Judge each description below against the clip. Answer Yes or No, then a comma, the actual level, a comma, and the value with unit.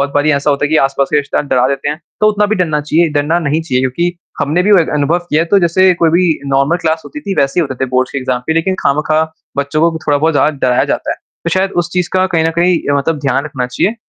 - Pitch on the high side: No, medium, 155 Hz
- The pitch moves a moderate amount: Yes, average, 3.6 semitones